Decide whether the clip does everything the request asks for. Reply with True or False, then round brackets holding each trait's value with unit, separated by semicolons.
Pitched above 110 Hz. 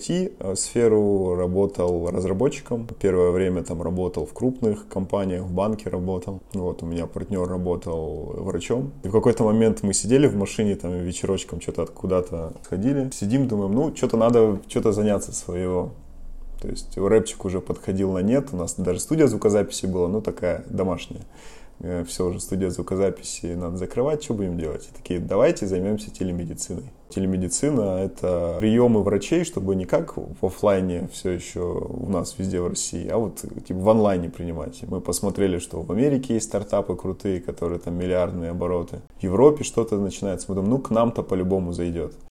False (95 Hz)